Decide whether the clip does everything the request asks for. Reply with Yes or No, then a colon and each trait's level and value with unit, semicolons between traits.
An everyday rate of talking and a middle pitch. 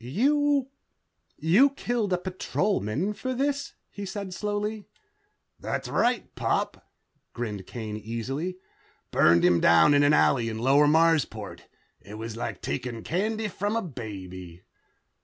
No: slow, 130 wpm; medium, 160 Hz